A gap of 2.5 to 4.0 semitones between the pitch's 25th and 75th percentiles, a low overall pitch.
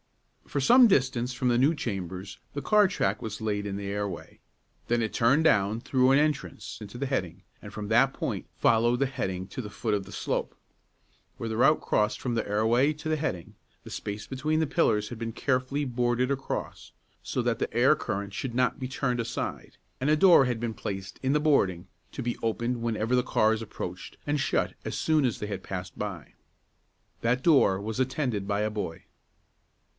No: average, 4.6 semitones; low, 120 Hz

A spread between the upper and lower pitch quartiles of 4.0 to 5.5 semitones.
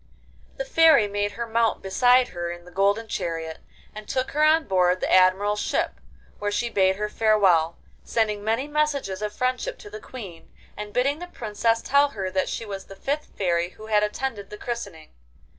Yes: average, 4.8 semitones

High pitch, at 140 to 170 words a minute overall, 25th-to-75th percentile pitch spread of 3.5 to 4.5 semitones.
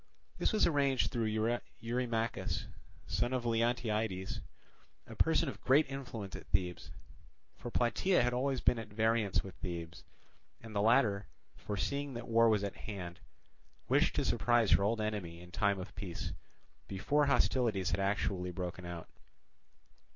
No: low, 110 Hz; average, 145 wpm; average, 4.0 semitones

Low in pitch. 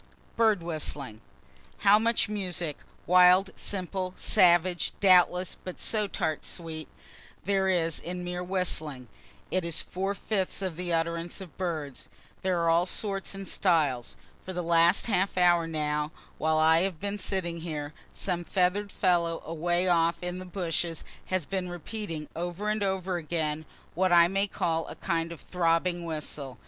No: medium, 175 Hz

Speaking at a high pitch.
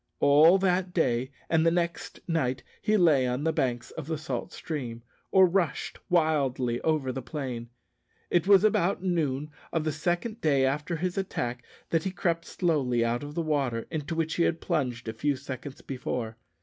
No: medium, 150 Hz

